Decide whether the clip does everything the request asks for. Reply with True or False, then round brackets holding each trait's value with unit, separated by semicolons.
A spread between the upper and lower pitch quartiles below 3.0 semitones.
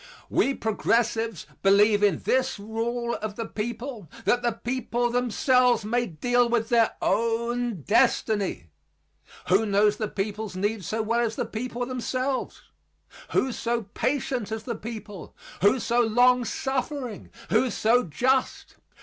True (2.4 semitones)